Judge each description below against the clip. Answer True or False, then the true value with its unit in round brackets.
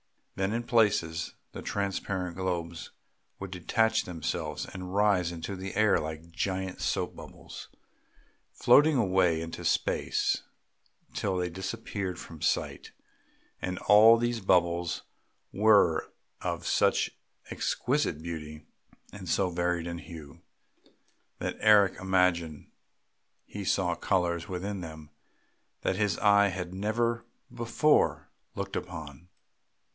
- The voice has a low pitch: True (95 Hz)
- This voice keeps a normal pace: False (115 wpm)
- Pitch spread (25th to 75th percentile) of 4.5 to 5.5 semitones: False (3.2 semitones)